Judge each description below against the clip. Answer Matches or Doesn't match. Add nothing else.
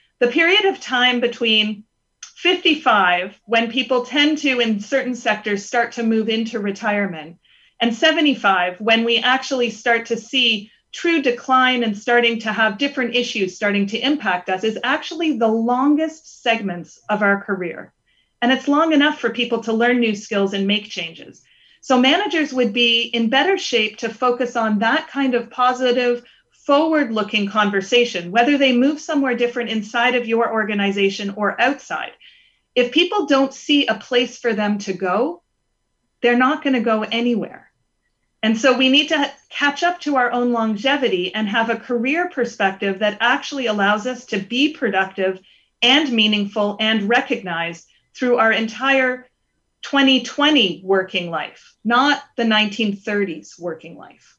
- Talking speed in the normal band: Matches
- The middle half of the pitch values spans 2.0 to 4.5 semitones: Matches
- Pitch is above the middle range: Matches